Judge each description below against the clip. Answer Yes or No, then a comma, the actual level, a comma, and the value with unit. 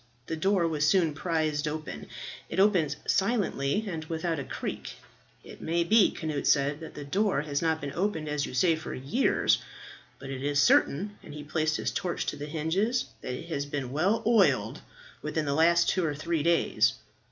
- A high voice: No, medium, 160 Hz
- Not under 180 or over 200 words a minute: Yes, average, 190 wpm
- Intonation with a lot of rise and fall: No, average, 3.3 semitones